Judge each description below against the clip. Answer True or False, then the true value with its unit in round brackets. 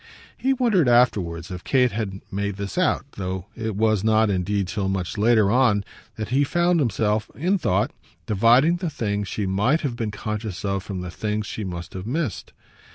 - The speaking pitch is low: True (105 Hz)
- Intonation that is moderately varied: True (4.1 semitones)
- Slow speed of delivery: False (185 wpm)